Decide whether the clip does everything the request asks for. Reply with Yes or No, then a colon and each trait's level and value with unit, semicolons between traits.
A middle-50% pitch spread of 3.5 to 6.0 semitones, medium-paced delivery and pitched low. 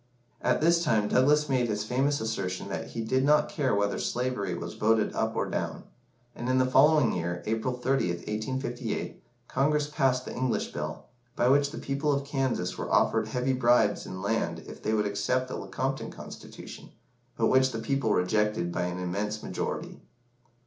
Yes: average, 4.2 semitones; average, 175 wpm; low, 120 Hz